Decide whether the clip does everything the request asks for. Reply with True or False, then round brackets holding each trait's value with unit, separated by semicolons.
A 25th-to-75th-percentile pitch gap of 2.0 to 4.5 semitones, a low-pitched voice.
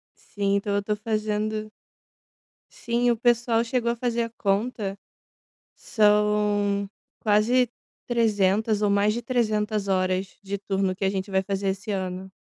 False (2.4 semitones; 210 Hz)